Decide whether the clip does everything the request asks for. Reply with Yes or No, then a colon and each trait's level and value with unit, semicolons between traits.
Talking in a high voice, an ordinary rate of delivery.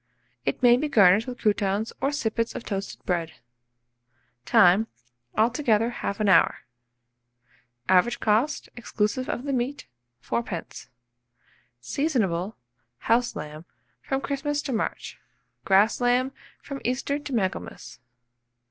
No: high, 230 Hz; slow, 110 wpm